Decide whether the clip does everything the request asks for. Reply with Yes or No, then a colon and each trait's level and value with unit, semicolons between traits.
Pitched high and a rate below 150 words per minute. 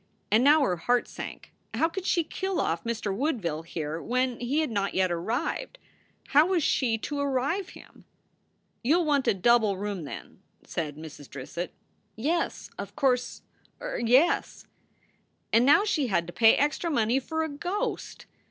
No: very high, 250 Hz; average, 165 wpm